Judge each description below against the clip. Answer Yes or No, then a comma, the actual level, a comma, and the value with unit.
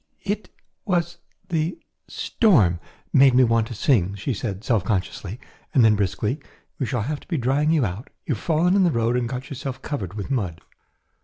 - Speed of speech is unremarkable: Yes, average, 190 wpm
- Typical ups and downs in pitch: No, wide, 6.5 semitones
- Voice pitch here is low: Yes, low, 125 Hz